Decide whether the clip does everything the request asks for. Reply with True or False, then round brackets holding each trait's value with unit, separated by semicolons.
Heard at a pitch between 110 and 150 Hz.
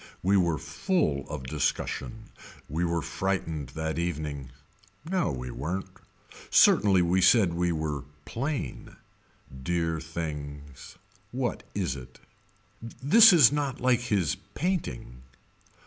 False (85 Hz)